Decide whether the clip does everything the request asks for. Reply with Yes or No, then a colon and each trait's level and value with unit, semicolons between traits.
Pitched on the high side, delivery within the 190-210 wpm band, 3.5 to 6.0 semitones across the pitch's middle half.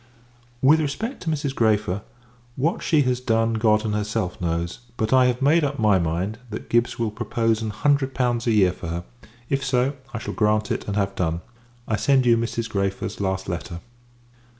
No: low, 115 Hz; average, 195 wpm; average, 4.2 semitones